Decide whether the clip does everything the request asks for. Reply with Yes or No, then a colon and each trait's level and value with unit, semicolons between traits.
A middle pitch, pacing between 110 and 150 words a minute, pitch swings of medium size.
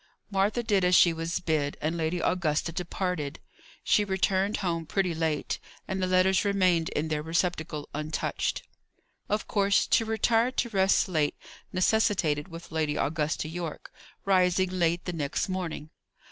Yes: medium, 175 Hz; average, 145 wpm; average, 3.2 semitones